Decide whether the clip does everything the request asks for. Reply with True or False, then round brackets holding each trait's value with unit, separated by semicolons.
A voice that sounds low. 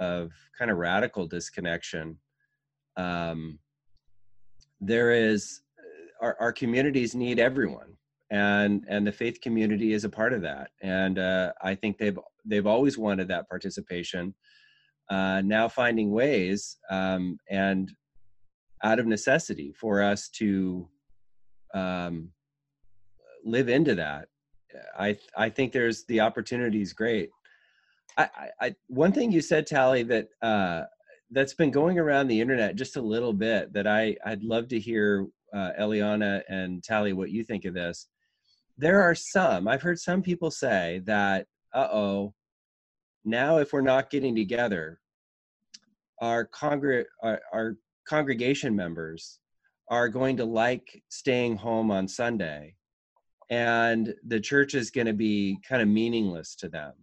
True (110 Hz)